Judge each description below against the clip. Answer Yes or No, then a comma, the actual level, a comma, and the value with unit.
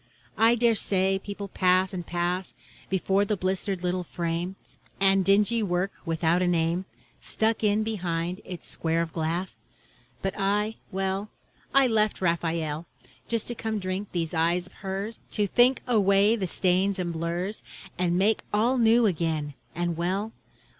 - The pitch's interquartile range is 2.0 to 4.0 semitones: Yes, average, 3.2 semitones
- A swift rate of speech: No, average, 155 wpm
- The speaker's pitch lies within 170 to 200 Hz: Yes, high, 190 Hz